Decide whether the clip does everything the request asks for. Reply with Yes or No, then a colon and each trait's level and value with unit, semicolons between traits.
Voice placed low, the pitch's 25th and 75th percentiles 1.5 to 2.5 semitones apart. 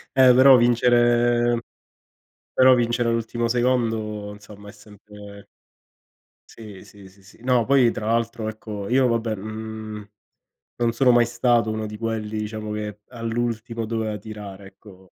Yes: low, 110 Hz; narrow, 2.1 semitones